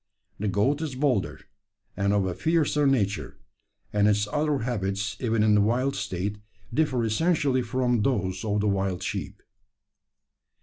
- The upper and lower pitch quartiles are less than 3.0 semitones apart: No, average, 4.9 semitones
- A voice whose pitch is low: Yes, low, 110 Hz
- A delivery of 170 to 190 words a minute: No, average, 145 wpm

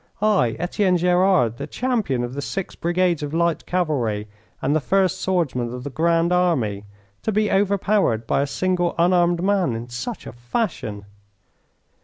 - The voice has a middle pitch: Yes, medium, 170 Hz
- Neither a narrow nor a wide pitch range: No, wide, 6.9 semitones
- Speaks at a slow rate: No, average, 160 wpm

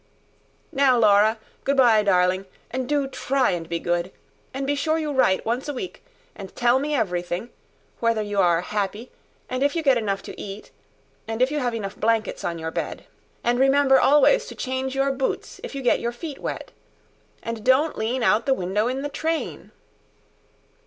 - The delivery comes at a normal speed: Yes, average, 190 wpm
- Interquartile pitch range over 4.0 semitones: Yes, average, 4.9 semitones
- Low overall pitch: No, high, 240 Hz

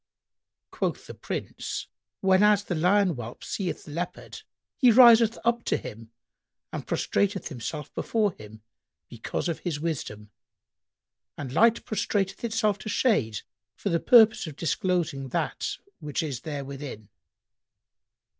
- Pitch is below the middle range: No, medium, 175 Hz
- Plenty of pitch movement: Yes, wide, 7.2 semitones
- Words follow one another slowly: Yes, slow, 125 wpm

